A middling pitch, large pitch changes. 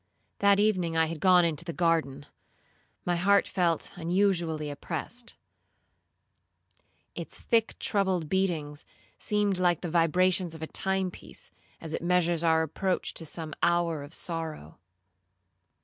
No: medium, 170 Hz; narrow, 2.6 semitones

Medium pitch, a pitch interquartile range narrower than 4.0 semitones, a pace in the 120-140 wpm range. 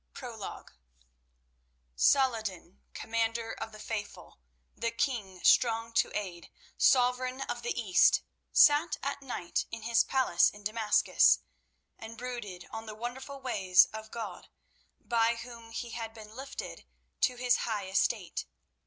No: high, 230 Hz; average, 2.7 semitones; slow, 135 wpm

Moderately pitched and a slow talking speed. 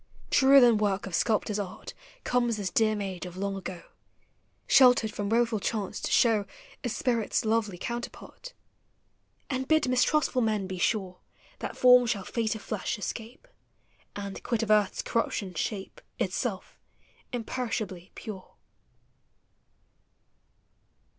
No: high, 220 Hz; slow, 125 wpm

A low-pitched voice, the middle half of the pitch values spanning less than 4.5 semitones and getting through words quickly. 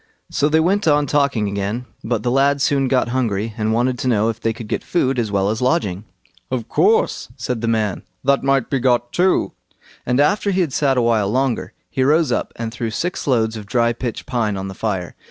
Yes: low, 120 Hz; average, 3.9 semitones; fast, 225 wpm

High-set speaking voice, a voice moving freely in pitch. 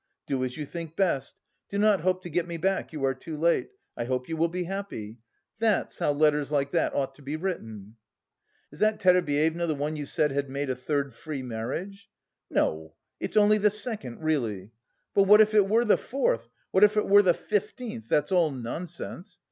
No: medium, 160 Hz; wide, 6.3 semitones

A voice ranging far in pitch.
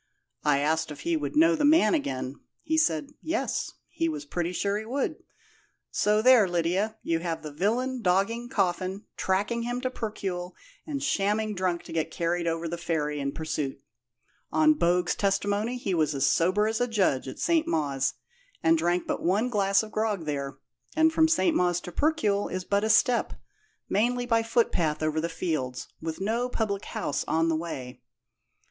Yes: wide, 5.8 semitones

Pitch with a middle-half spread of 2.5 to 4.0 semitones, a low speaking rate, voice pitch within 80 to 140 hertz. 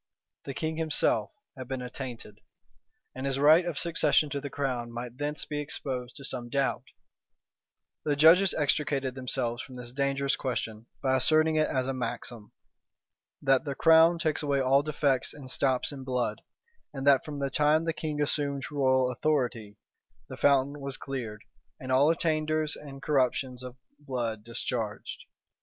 No: average, 2.8 semitones; average, 160 wpm; low, 135 Hz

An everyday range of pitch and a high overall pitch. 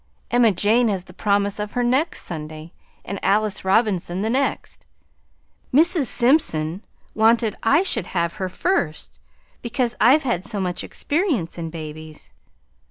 No: wide, 5.8 semitones; high, 210 Hz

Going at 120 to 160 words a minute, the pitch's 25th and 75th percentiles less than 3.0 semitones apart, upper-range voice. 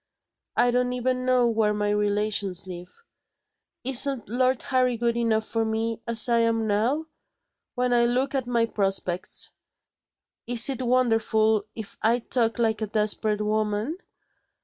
Yes: average, 145 wpm; narrow, 2.5 semitones; high, 230 Hz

